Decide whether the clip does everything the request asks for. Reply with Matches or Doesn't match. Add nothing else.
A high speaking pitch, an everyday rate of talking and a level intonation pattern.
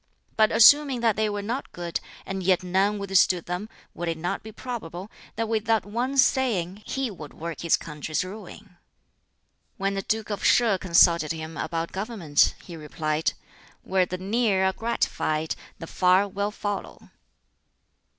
Doesn't match